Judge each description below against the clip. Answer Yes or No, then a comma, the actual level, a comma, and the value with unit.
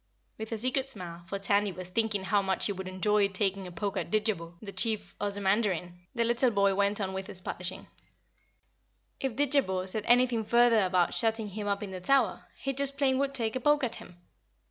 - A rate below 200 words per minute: No, fast, 205 wpm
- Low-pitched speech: No, high, 205 Hz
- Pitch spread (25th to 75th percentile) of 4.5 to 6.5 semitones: No, average, 3.8 semitones